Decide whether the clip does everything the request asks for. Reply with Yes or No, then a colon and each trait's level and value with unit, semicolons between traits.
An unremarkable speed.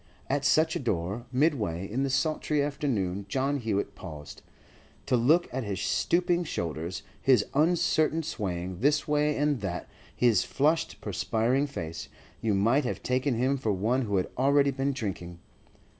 Yes: average, 155 wpm